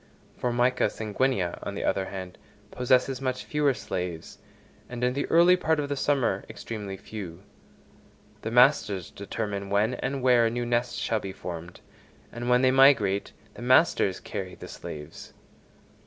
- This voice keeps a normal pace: Yes, average, 155 wpm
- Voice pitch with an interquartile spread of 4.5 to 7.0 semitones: Yes, average, 4.8 semitones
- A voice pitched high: No, low, 120 Hz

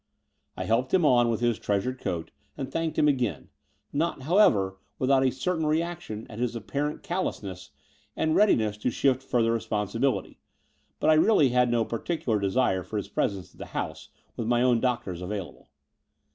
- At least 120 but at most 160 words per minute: No, average, 170 wpm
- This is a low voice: Yes, low, 120 Hz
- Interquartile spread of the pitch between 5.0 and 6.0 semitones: Yes, wide, 5.6 semitones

